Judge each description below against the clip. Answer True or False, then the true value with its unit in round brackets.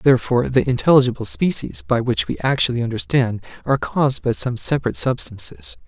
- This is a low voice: True (130 Hz)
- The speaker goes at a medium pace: True (155 wpm)